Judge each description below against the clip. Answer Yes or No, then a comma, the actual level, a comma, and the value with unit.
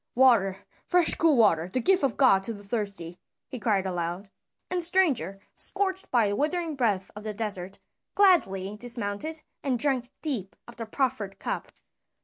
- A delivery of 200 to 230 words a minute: No, average, 165 wpm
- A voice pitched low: No, high, 230 Hz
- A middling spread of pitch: No, wide, 6.5 semitones